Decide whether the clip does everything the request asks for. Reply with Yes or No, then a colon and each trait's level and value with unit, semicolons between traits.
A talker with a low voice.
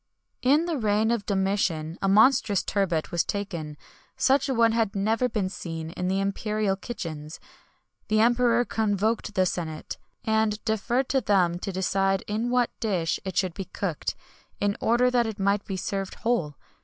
No: high, 205 Hz